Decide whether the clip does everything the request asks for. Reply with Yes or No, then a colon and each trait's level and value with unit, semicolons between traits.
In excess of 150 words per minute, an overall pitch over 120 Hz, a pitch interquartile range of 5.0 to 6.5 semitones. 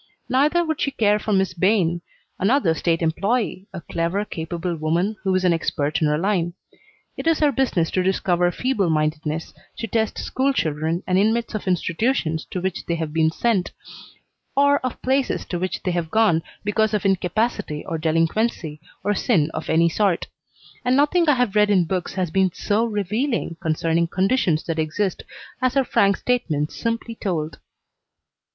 Yes: average, 170 wpm; high, 190 Hz; average, 5.3 semitones